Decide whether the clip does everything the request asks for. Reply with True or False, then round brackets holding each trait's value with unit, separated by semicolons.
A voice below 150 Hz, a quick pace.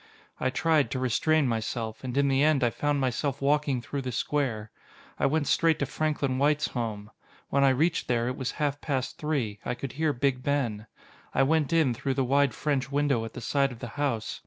True (135 Hz; 210 wpm)